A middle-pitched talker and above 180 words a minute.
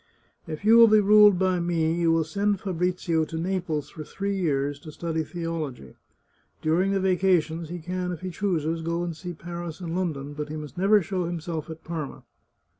Yes: medium, 170 Hz; average, 195 wpm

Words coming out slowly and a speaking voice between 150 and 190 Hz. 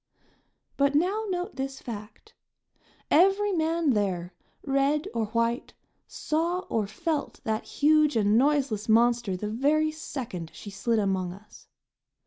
No: slow, 125 wpm; very high, 265 Hz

